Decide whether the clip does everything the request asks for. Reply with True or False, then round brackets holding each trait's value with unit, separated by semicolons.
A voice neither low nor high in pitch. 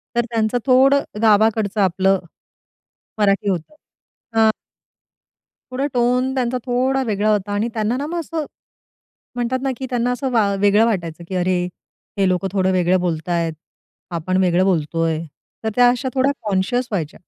False (215 Hz)